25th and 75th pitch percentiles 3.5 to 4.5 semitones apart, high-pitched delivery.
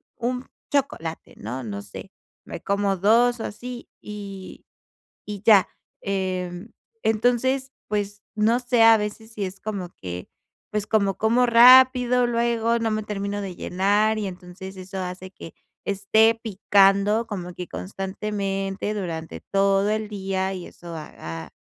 No: average, 3.1 semitones; high, 205 Hz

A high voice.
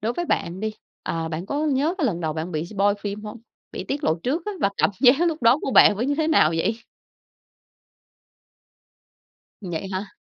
Yes: high, 210 Hz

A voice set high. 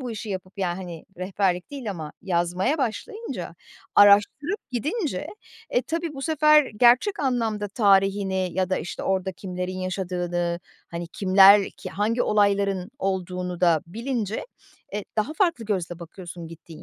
Yes: high, 195 Hz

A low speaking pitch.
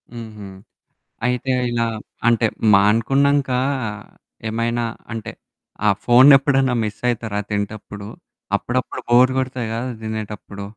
Yes: low, 115 Hz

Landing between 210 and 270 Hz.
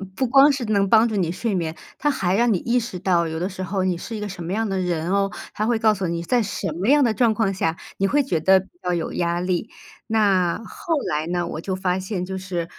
No: high, 190 Hz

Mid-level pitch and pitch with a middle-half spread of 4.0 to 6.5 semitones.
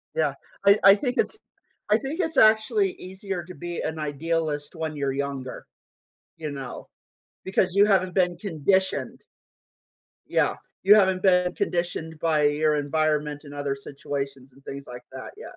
Yes: medium, 160 Hz; average, 4.7 semitones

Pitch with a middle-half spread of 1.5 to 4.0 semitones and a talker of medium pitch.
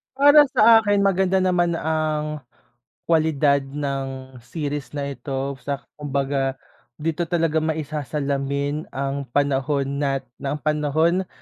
Yes: narrow, 2.6 semitones; medium, 145 Hz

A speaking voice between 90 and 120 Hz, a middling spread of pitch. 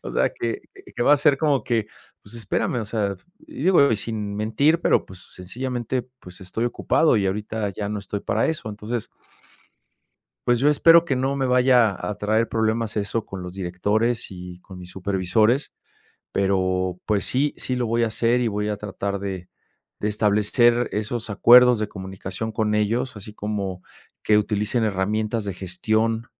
Yes: low, 110 Hz; average, 3.3 semitones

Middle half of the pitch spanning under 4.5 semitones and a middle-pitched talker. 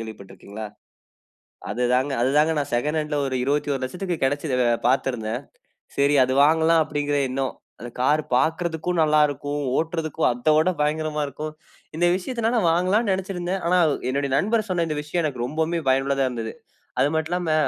Yes: average, 3.7 semitones; medium, 150 Hz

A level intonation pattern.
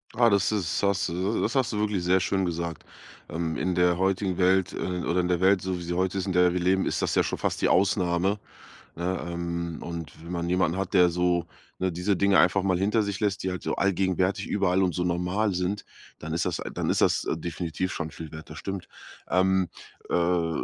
Yes: narrow, 1.8 semitones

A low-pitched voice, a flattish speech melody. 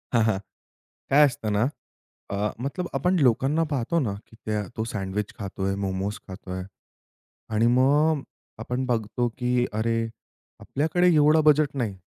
No: low, 120 Hz; wide, 5.6 semitones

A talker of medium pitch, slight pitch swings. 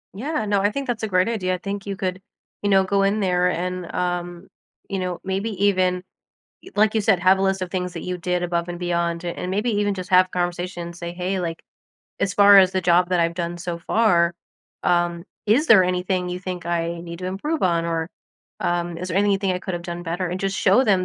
Yes: medium, 180 Hz; narrow, 2.0 semitones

